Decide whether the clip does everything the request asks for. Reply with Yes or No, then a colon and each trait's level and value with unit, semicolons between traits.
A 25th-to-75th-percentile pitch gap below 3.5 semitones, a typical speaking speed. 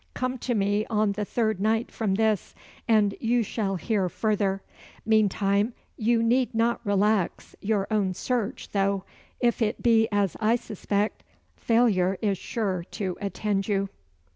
Yes: narrow, 2.4 semitones; average, 145 wpm